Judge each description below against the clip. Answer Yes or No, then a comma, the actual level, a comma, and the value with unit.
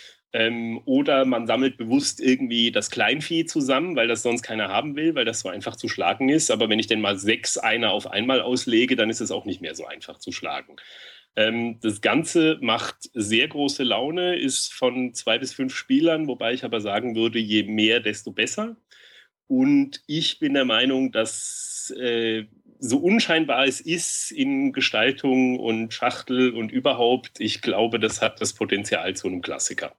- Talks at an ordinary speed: Yes, average, 180 wpm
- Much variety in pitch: Yes, wide, 5.9 semitones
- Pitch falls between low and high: No, low, 125 Hz